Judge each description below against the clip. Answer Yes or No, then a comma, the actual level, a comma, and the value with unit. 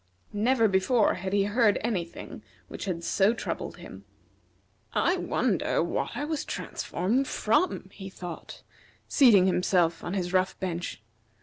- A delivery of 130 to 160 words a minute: Yes, average, 140 wpm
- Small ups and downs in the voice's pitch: No, average, 4.0 semitones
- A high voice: Yes, high, 195 Hz